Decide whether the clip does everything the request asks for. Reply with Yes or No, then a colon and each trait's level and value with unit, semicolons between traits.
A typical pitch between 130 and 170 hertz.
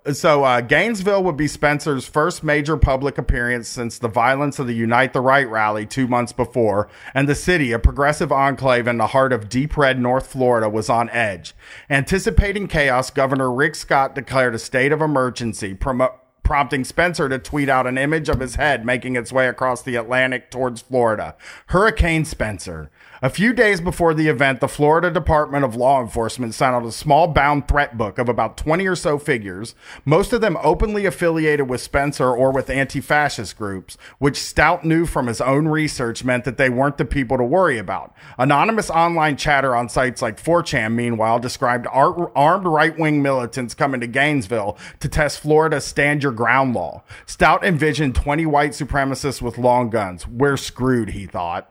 Yes: low, 135 Hz